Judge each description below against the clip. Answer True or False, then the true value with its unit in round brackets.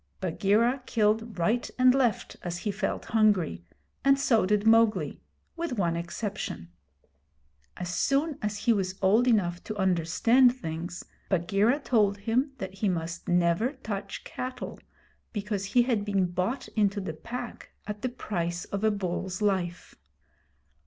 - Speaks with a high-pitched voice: True (205 Hz)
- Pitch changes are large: False (4.5 semitones)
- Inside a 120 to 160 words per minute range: True (145 wpm)